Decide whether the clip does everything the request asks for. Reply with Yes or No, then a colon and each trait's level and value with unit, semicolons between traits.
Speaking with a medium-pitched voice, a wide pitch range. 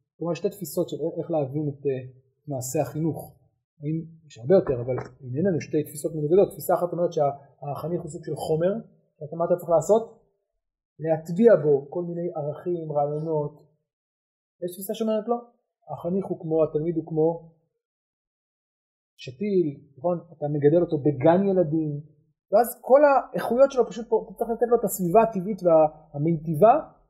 No: medium, 165 Hz; average, 4.2 semitones